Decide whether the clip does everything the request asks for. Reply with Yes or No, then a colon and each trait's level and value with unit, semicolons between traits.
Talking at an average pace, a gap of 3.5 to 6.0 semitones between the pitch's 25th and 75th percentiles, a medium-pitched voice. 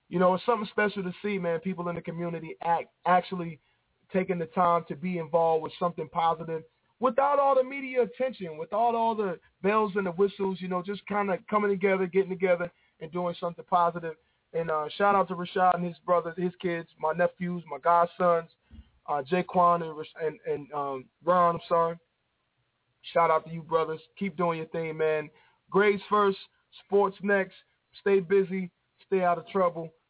No: average, 185 wpm; average, 2.8 semitones; medium, 175 Hz